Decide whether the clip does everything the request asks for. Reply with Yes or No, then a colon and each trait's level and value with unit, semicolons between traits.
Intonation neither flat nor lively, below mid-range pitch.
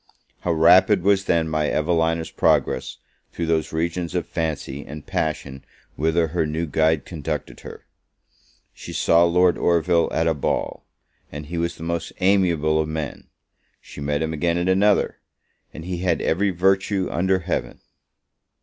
No: narrow, 2.2 semitones; very low, 85 Hz